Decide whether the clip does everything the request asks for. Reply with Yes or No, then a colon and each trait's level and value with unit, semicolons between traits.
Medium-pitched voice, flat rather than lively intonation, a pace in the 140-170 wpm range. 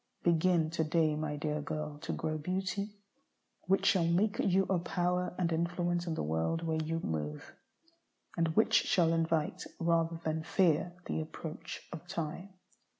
Yes: medium, 165 Hz; narrow, 2.1 semitones; average, 160 wpm